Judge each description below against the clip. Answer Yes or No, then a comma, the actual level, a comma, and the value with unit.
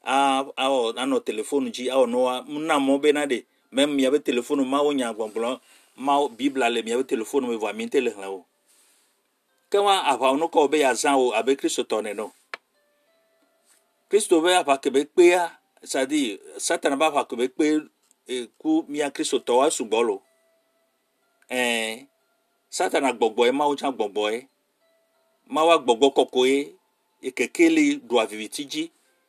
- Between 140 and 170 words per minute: Yes, average, 150 wpm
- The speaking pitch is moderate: Yes, medium, 160 Hz